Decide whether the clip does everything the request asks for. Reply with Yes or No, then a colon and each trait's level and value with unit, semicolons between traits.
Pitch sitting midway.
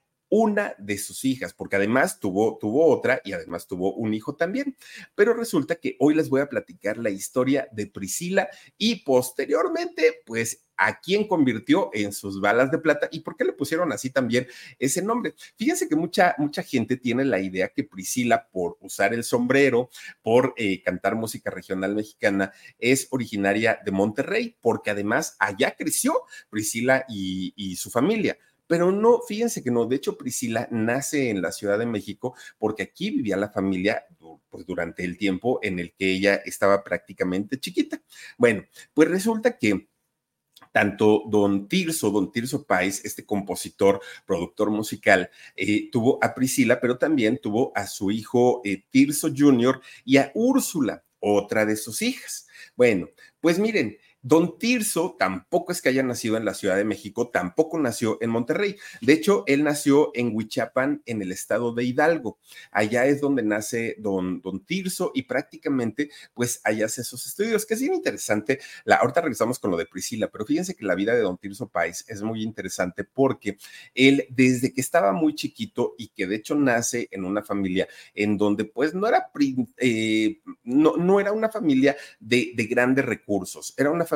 No: low, 130 Hz